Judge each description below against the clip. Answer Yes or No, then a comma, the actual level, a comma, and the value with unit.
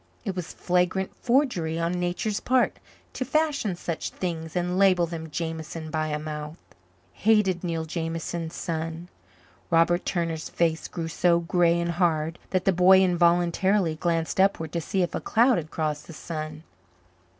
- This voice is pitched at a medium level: Yes, medium, 170 Hz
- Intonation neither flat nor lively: No, narrow, 2.2 semitones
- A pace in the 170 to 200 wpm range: No, average, 155 wpm